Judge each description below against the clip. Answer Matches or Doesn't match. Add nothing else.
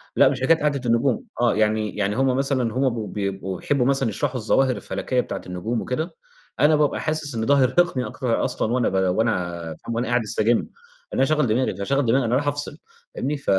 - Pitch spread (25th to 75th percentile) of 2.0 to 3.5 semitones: Doesn't match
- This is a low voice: Matches